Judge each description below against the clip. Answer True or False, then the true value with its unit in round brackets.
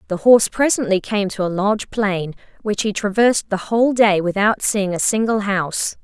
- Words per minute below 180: False (190 wpm)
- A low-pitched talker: False (200 Hz)